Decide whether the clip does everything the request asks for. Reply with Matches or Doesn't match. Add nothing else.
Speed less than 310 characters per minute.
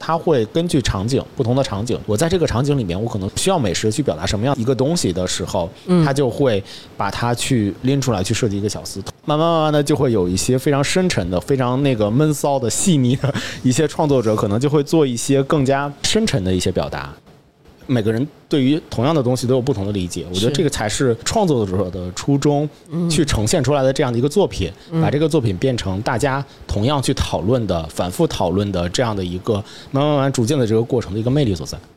Doesn't match